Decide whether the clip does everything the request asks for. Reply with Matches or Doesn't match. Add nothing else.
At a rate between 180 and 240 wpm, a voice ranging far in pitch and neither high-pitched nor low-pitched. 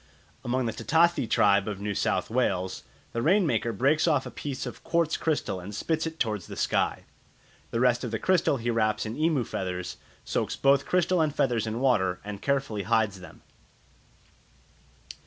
Doesn't match